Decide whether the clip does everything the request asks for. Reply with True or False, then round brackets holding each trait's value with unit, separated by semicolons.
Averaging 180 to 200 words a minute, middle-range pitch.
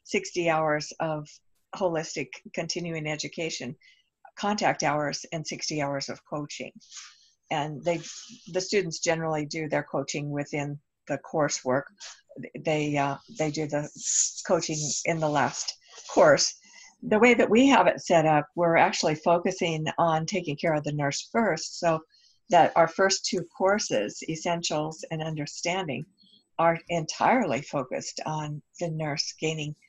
False (135 wpm; 160 Hz)